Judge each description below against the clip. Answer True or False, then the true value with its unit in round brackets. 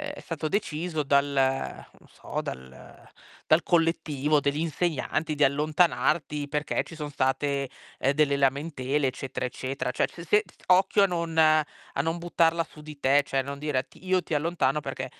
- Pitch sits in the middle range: True (150 Hz)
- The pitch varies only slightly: False (3.0 semitones)